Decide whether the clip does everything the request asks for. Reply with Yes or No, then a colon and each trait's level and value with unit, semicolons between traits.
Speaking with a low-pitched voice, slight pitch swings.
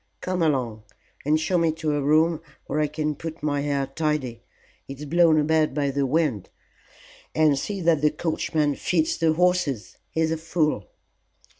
No: medium, 155 Hz; narrow, 2.3 semitones